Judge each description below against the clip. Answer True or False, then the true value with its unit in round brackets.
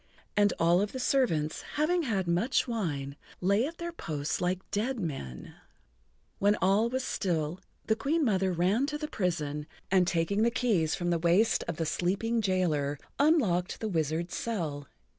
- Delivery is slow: False (170 wpm)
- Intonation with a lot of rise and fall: True (5.8 semitones)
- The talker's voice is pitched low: False (185 Hz)